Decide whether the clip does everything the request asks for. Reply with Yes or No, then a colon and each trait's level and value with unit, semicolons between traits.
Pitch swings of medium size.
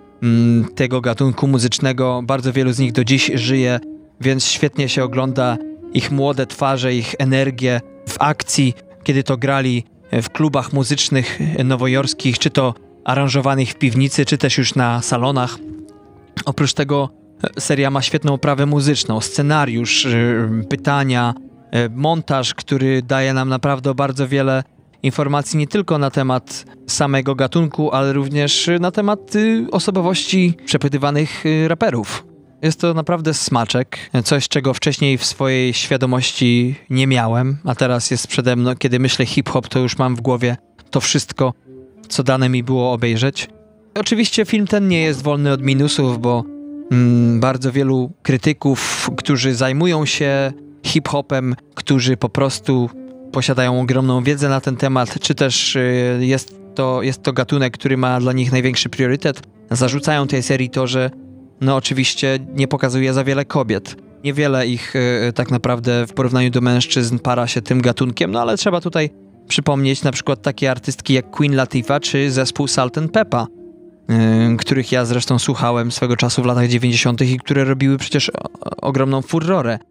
No: narrow, 2.3 semitones